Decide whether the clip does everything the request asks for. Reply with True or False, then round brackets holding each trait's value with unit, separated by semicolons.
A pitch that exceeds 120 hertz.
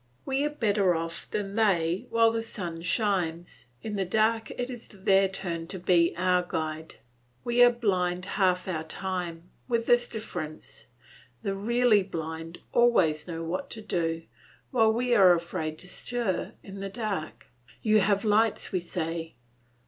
True (190 Hz)